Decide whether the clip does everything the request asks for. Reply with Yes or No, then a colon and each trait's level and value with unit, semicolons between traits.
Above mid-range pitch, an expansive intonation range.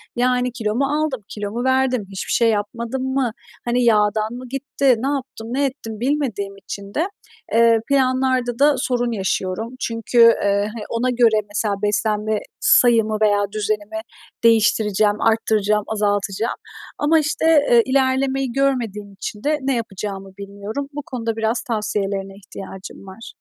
No: high, 230 Hz; average, 3.7 semitones